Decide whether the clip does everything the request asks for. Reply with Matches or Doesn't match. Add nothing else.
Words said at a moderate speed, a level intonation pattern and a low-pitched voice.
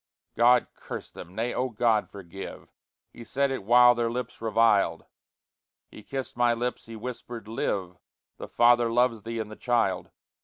Matches